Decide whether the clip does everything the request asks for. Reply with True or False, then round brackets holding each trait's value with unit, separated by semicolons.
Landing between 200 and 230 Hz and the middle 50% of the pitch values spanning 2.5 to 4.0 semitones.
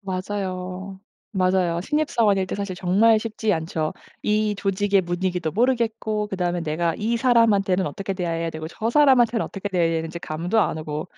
False (190 Hz; 3.6 semitones)